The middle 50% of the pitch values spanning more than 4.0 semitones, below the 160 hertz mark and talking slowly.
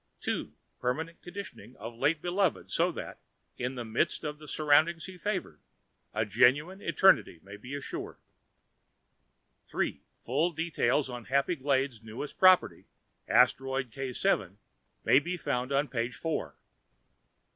Yes: average, 5.2 semitones; medium, 140 Hz; slow, 125 wpm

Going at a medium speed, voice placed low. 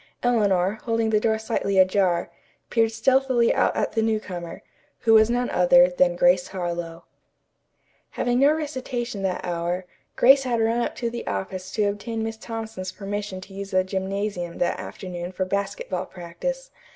No: average, 165 wpm; high, 200 Hz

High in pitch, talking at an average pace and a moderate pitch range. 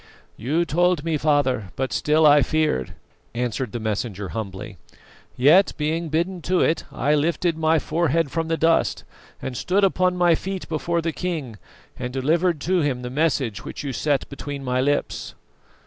No: medium, 150 Hz; average, 165 wpm; average, 4.5 semitones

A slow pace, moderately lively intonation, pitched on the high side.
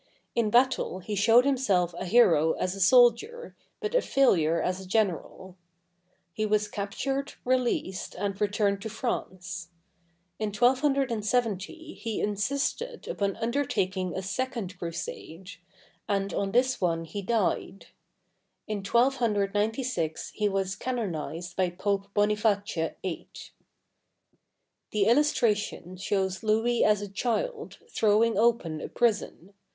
Yes: slow, 120 wpm; average, 4.2 semitones; high, 210 Hz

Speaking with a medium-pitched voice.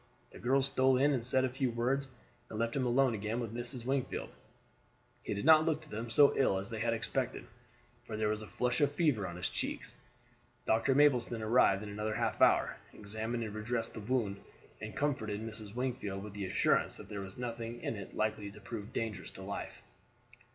No: low, 115 Hz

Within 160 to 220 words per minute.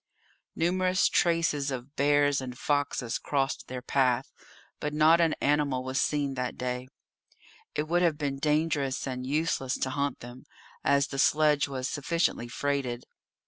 No: average, 145 wpm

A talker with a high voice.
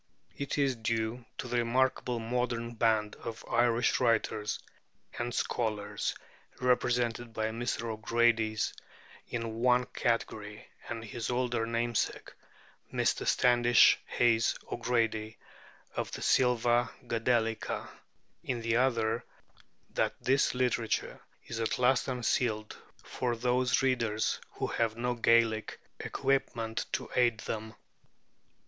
No: low, 115 Hz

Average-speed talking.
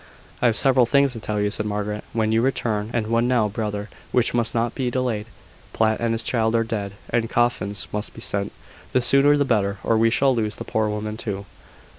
No: fast, 220 wpm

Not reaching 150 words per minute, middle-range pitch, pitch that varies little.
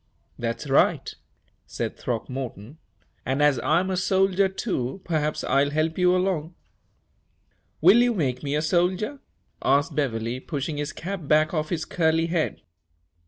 No: average, 140 wpm; medium, 155 Hz; average, 4.5 semitones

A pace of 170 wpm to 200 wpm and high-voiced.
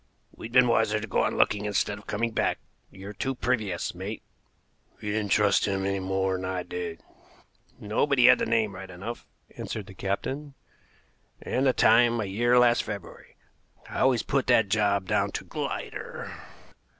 No: average, 175 wpm; low, 105 Hz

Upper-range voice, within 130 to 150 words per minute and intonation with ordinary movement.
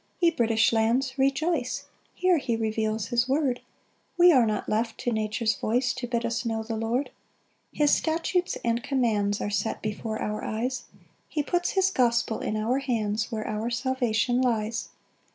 No: high, 235 Hz; average, 170 wpm; average, 3.2 semitones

